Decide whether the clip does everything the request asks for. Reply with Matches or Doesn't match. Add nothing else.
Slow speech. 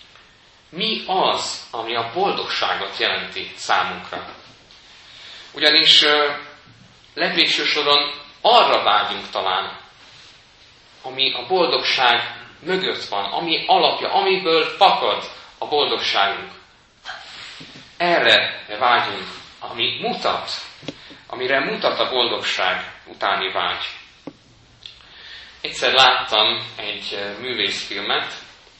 Matches